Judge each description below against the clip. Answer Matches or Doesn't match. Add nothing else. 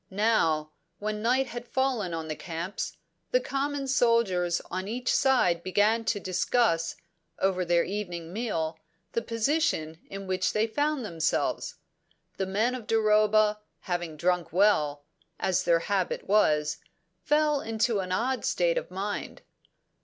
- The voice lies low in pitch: Doesn't match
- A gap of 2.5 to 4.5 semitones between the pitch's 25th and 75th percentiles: Doesn't match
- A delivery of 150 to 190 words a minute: Doesn't match